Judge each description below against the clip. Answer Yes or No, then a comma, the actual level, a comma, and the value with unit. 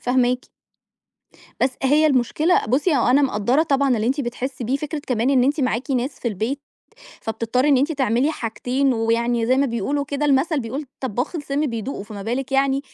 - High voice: Yes, very high, 260 Hz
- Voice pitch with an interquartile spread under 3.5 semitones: Yes, average, 2.9 semitones